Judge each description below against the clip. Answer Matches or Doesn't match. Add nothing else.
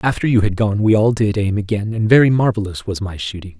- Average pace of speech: Doesn't match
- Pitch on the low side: Matches